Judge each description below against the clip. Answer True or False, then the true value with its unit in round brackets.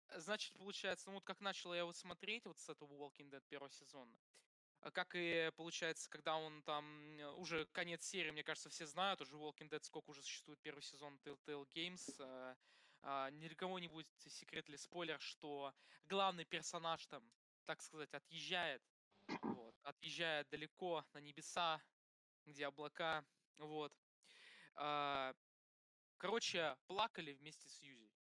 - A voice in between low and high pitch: True (155 Hz)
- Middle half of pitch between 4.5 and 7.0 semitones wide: False (3.2 semitones)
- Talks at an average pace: True (150 wpm)